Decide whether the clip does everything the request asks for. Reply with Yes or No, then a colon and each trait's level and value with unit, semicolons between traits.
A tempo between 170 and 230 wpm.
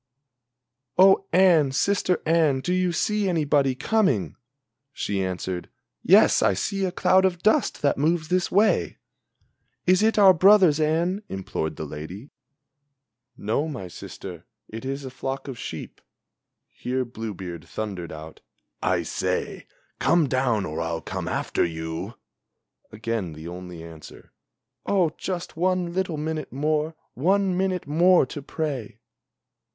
No: slow, 135 wpm